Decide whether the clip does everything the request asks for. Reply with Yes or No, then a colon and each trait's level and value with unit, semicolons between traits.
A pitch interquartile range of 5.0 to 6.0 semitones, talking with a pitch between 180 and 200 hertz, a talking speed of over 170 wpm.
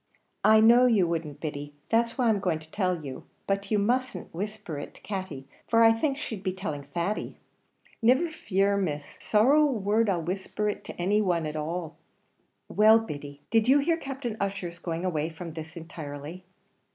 Yes: wide, 5.6 semitones; high, 190 Hz; average, 190 wpm